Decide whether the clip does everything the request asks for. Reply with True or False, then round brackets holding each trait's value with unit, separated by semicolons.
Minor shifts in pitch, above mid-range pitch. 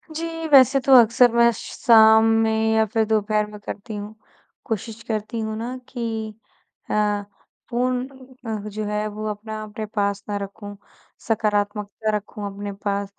True (1.6 semitones; 215 Hz)